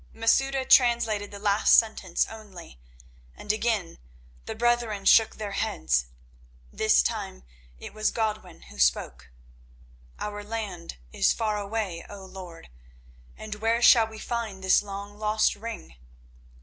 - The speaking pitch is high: Yes, high, 210 Hz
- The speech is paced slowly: Yes, slow, 130 wpm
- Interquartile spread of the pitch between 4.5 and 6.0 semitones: No, average, 2.8 semitones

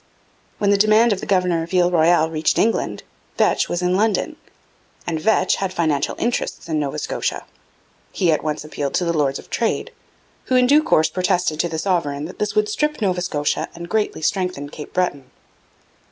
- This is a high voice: No, medium, 180 Hz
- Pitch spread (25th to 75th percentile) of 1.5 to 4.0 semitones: No, average, 4.5 semitones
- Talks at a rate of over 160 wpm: Yes, average, 190 wpm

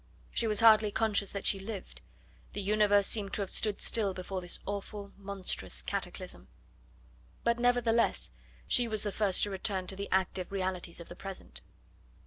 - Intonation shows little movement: Yes, narrow, 2.1 semitones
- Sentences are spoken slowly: No, average, 165 wpm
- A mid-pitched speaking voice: No, high, 200 Hz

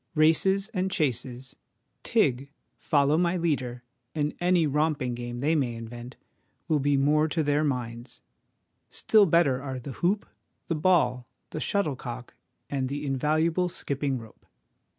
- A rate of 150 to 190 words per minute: No, slow, 135 wpm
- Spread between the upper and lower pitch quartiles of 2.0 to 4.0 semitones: No, average, 4.4 semitones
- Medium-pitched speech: Yes, medium, 145 Hz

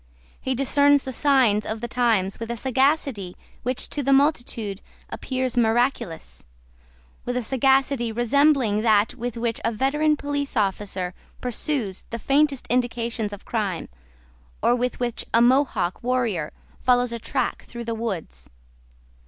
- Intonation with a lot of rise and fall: No, average, 3.5 semitones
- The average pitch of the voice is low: No, high, 240 Hz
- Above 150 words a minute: No, average, 140 wpm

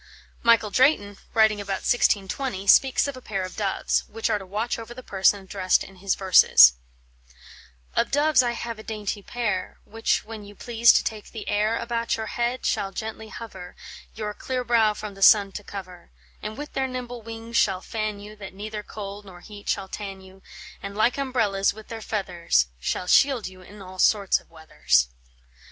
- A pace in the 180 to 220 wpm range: Yes, average, 190 wpm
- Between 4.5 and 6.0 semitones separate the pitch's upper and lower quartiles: No, average, 3.0 semitones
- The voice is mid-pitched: No, high, 210 Hz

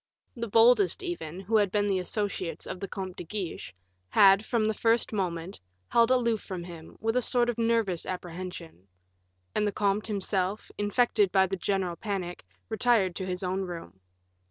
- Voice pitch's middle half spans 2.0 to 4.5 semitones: Yes, average, 3.7 semitones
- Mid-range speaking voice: No, high, 195 Hz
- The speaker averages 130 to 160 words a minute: No, average, 175 wpm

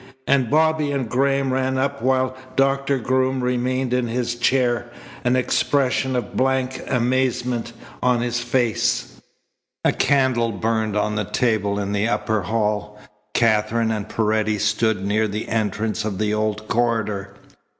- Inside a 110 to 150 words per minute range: Yes, average, 140 wpm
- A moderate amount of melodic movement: Yes, average, 3.3 semitones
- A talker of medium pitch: No, low, 120 Hz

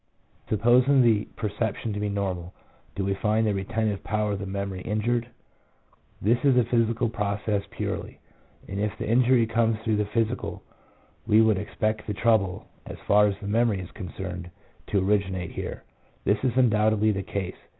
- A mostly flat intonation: Yes, narrow, 2.3 semitones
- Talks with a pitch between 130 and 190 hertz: No, low, 105 Hz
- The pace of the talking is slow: No, average, 170 wpm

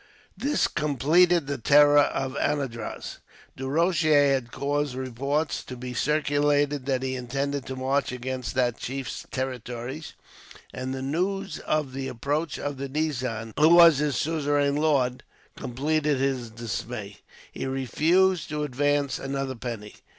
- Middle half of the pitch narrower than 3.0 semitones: Yes, narrow, 2.6 semitones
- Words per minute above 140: No, slow, 135 wpm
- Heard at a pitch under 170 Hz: Yes, medium, 140 Hz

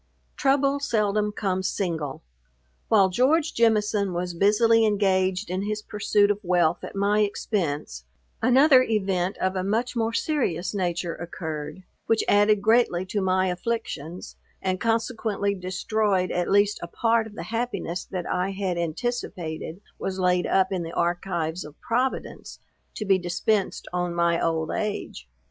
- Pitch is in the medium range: No, high, 195 Hz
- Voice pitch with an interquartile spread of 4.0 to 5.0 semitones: No, average, 3.6 semitones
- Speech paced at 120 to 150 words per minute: Yes, average, 145 wpm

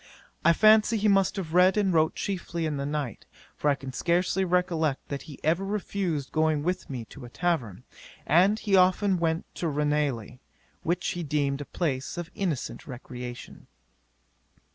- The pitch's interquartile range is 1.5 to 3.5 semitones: No, average, 4.5 semitones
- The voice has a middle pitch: Yes, medium, 160 Hz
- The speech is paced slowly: No, average, 165 wpm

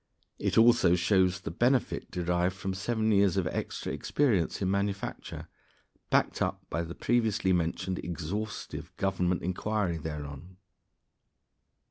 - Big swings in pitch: No, average, 3.3 semitones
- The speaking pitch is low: Yes, very low, 95 Hz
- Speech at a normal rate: No, slow, 115 wpm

